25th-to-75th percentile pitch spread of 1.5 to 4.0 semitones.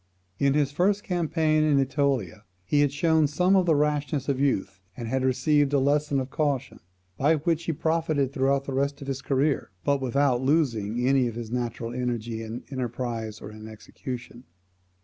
Yes: average, 3.3 semitones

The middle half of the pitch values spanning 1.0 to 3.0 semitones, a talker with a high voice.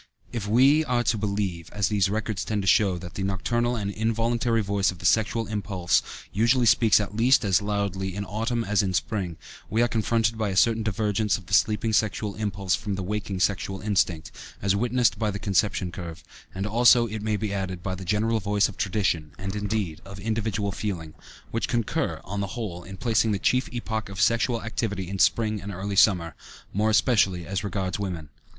No: narrow, 2.6 semitones; low, 105 Hz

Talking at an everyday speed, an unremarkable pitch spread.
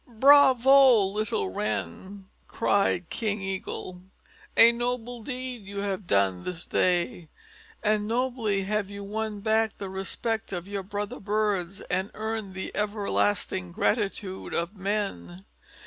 No: slow, 125 wpm; average, 3.0 semitones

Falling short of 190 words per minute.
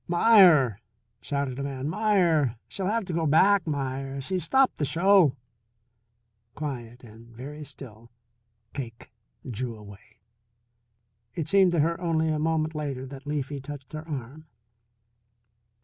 Yes: slow, 135 wpm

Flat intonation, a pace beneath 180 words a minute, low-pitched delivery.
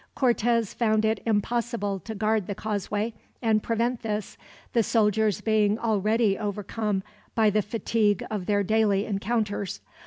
No: narrow, 1.7 semitones; slow, 135 wpm; high, 215 Hz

